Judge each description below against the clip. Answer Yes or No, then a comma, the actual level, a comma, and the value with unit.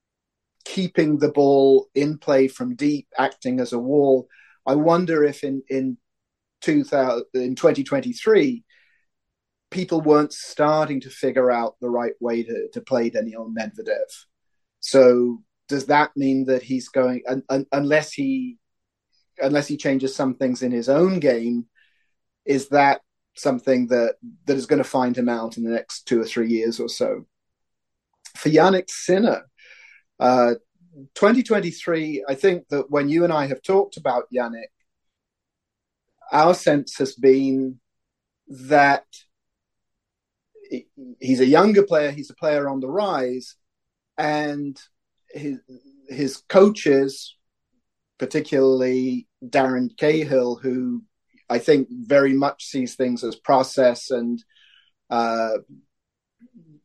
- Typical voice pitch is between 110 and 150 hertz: Yes, low, 135 Hz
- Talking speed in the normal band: No, slow, 130 wpm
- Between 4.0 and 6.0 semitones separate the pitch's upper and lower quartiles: No, average, 3.6 semitones